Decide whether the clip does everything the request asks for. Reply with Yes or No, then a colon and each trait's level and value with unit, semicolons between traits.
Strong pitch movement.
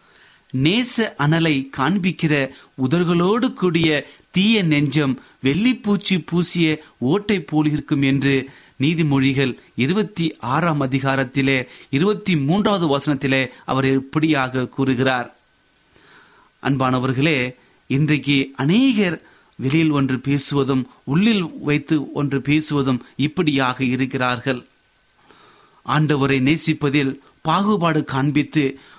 No: average, 3.5 semitones